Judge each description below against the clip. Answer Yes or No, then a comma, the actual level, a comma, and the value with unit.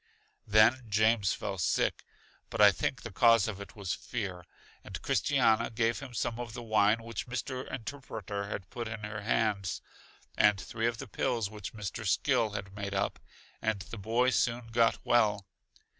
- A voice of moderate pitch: No, low, 110 Hz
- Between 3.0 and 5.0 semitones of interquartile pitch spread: No, narrow, 2.4 semitones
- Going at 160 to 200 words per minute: Yes, average, 175 wpm